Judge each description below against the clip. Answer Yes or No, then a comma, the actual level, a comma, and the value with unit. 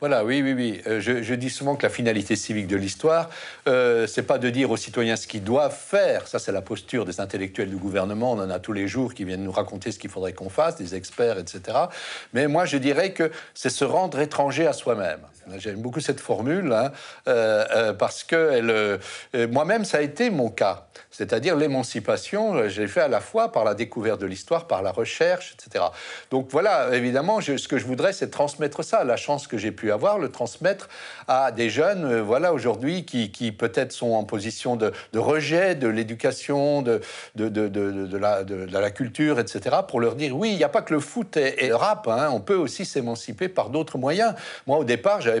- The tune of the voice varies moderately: No, wide, 6.3 semitones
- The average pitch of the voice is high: No, low, 125 Hz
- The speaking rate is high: Yes, fast, 225 wpm